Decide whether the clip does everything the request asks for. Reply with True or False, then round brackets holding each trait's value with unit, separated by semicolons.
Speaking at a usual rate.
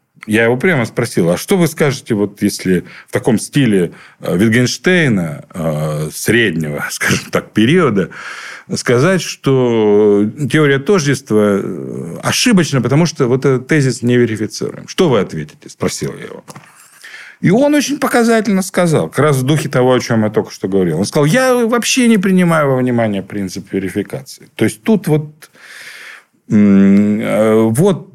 True (145 wpm)